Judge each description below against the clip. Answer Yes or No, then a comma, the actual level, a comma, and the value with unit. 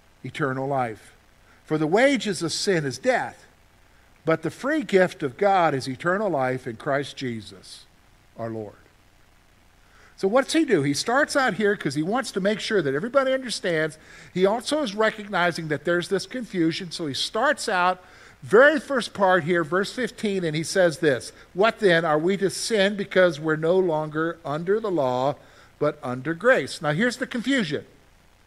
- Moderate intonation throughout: No, wide, 7.6 semitones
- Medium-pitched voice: Yes, medium, 170 Hz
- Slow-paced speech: No, average, 175 wpm